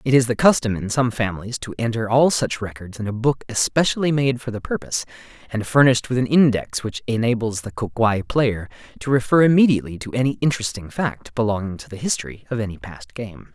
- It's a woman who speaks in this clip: No, male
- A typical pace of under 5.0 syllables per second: No, 6.0 syllables/s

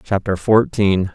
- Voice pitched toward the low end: Yes, low, 100 Hz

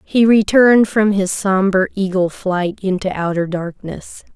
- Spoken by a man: No, female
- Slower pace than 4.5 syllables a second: Yes, 4.2 syllables/s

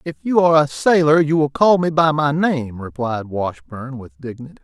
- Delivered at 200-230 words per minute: Yes, fast, 205 wpm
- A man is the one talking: Yes, male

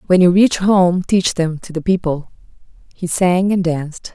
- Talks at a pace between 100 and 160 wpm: No, average, 190 wpm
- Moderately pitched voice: Yes, medium, 180 Hz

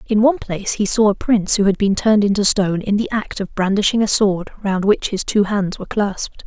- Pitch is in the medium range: No, high, 205 Hz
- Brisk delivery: Yes, fast, 250 wpm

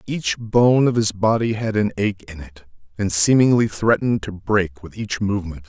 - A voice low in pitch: Yes, low, 105 Hz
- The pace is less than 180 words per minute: No, average, 190 wpm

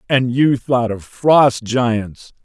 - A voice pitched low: Yes, low, 120 Hz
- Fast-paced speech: No, average, 150 wpm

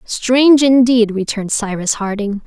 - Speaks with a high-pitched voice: Yes, high, 225 Hz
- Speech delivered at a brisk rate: No, slow, 120 wpm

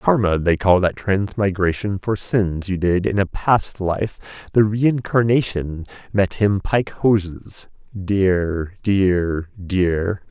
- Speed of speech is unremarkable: No, slow, 130 wpm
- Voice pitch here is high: No, very low, 95 Hz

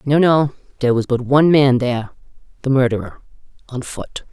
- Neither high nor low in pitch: No, low, 130 Hz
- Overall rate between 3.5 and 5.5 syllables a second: No, 5.8 syllables/s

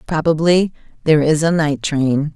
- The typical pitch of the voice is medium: Yes, medium, 155 Hz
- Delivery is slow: No, average, 155 wpm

